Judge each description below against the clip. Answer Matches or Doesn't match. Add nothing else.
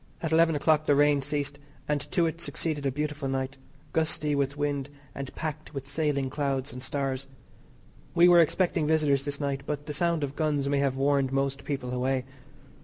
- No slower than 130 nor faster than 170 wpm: Doesn't match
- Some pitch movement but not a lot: Doesn't match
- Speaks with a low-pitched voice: Doesn't match